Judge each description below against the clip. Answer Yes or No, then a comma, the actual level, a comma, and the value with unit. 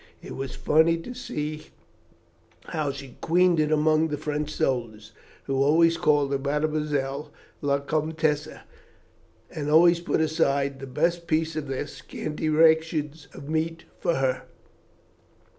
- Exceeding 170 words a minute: No, slow, 135 wpm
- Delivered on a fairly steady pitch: Yes, narrow, 2.2 semitones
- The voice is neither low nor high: Yes, medium, 150 Hz